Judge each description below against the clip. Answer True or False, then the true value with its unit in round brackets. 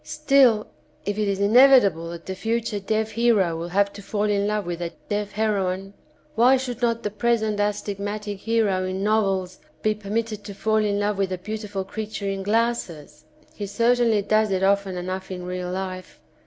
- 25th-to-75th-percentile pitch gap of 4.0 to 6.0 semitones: False (2.4 semitones)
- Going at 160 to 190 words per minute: True (185 wpm)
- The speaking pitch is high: True (205 Hz)